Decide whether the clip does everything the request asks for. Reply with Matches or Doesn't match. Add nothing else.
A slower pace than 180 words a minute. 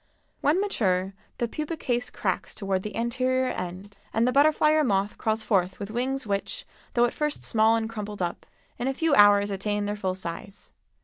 Doesn't match